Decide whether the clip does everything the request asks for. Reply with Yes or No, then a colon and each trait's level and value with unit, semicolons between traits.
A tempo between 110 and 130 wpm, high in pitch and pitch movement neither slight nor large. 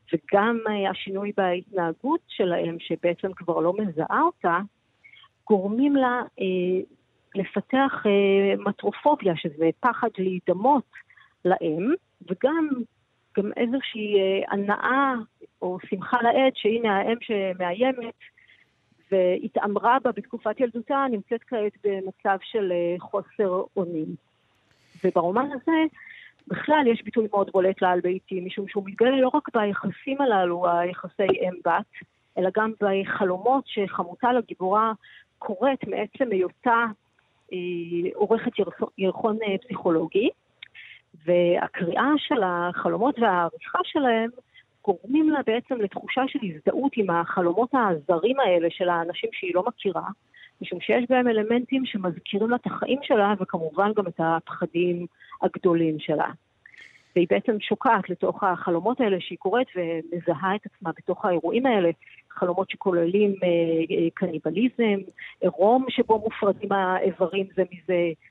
Yes: average, 115 wpm; high, 200 Hz; average, 4.8 semitones